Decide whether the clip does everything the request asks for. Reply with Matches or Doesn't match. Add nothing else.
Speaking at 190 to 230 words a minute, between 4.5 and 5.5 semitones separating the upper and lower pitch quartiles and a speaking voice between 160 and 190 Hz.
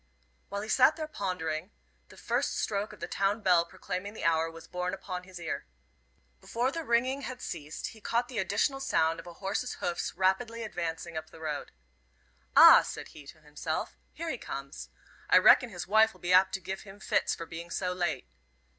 Matches